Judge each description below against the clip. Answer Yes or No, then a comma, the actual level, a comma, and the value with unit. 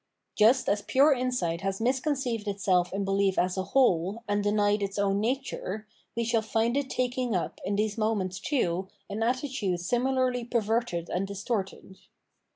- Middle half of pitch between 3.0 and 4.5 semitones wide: Yes, average, 4.1 semitones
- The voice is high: Yes, high, 215 Hz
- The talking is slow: No, average, 165 wpm